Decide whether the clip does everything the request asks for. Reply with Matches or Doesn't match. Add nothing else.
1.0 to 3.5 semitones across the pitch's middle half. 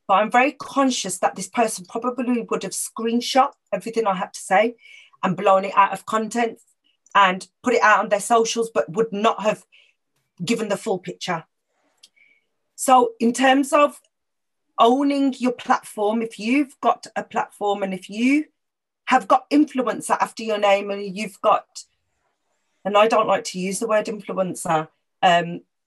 Doesn't match